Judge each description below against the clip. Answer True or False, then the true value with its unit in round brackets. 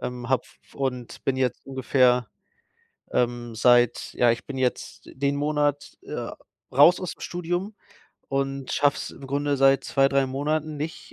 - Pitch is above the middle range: False (135 Hz)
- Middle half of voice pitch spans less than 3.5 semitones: True (2.6 semitones)